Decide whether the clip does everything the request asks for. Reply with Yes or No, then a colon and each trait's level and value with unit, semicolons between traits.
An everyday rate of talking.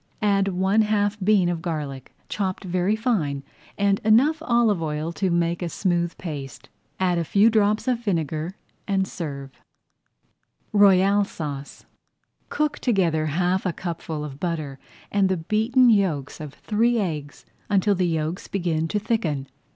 Yes: average, 150 wpm